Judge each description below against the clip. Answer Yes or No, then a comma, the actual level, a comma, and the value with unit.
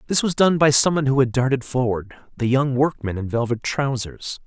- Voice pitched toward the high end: No, low, 130 Hz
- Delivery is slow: No, average, 200 wpm